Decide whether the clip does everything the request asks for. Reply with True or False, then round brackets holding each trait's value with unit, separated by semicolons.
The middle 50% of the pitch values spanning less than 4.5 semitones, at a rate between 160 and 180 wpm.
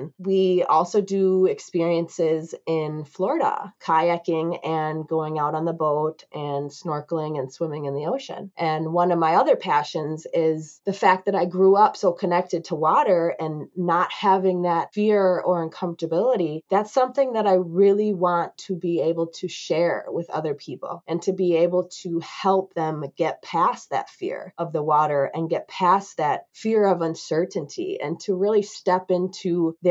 True (2.9 semitones; 170 wpm)